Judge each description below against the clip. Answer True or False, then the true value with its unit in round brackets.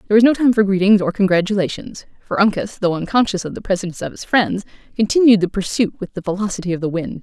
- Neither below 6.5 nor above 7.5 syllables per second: True (6.8 syllables/s)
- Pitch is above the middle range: True (200 Hz)